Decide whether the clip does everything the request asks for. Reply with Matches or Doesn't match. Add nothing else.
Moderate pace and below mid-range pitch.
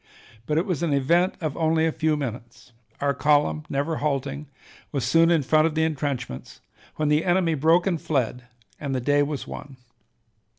Doesn't match